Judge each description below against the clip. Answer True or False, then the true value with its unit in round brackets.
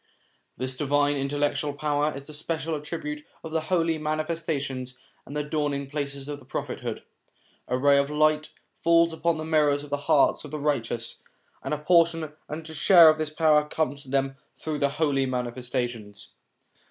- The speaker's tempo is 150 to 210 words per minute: True (175 wpm)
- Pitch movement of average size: False (2.1 semitones)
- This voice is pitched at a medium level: True (150 Hz)